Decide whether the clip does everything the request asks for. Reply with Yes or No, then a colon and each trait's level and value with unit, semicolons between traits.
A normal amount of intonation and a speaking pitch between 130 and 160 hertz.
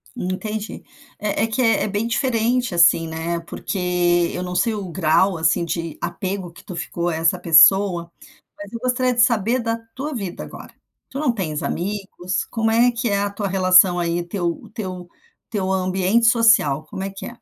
No: average, 4.5 semitones; high, 195 Hz